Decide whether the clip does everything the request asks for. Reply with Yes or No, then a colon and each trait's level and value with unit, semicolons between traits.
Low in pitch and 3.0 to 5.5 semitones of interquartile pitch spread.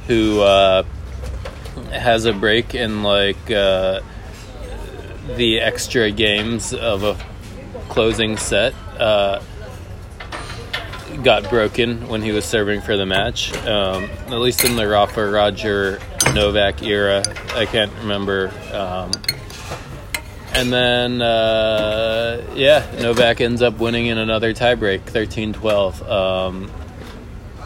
No: low, 105 Hz; narrow, 2.6 semitones